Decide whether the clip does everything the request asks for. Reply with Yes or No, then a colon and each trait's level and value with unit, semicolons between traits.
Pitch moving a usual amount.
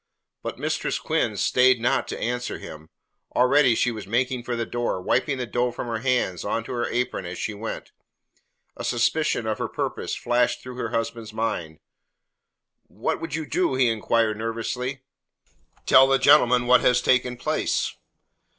No: narrow, 1.9 semitones